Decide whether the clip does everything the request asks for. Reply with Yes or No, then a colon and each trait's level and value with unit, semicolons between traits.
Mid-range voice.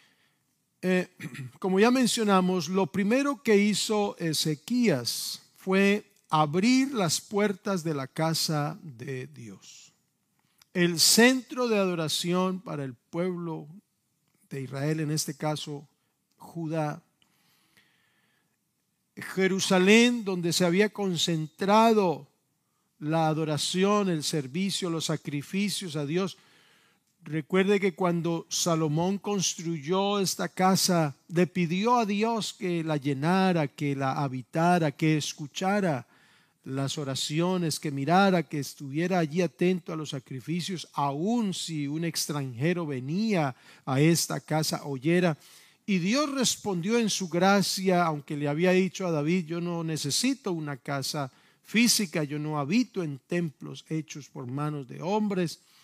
Yes: medium, 170 Hz